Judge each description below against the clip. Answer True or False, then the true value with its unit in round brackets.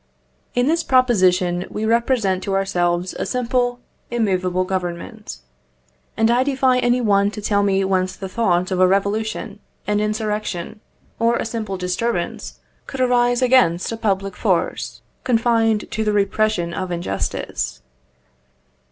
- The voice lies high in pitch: True (210 Hz)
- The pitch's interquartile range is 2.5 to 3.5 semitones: False (4.1 semitones)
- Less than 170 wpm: True (135 wpm)